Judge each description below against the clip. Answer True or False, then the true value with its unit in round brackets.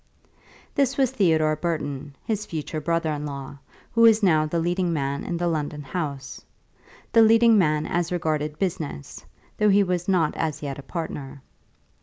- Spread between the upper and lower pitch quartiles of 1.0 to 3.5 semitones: False (3.9 semitones)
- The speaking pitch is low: False (165 Hz)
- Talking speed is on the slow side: False (165 wpm)